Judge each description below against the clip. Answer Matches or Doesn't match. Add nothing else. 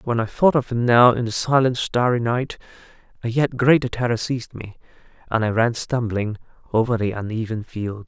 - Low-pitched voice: Matches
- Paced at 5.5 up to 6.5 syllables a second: Doesn't match